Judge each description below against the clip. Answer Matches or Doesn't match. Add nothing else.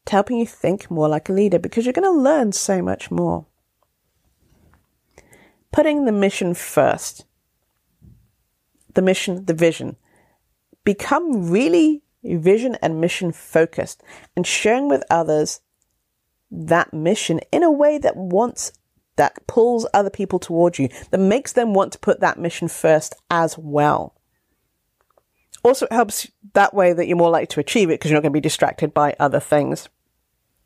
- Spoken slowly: Doesn't match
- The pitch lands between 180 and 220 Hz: Matches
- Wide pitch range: Matches